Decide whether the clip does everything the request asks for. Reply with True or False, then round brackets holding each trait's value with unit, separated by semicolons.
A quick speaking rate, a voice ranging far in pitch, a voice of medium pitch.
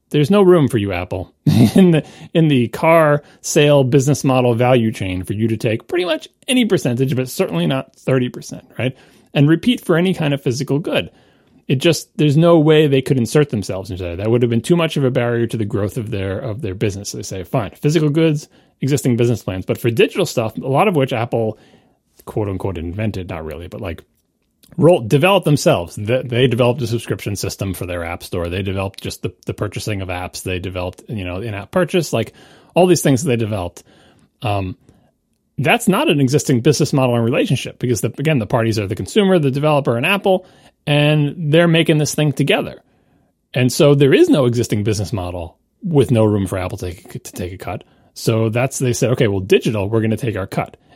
False (210 wpm; 5.7 semitones; 125 Hz)